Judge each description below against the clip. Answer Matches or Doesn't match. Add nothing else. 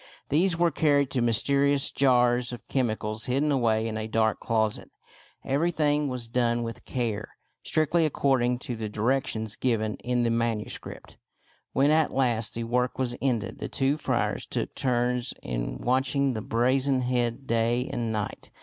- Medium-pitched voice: Doesn't match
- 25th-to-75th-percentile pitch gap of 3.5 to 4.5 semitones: Doesn't match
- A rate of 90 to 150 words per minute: Doesn't match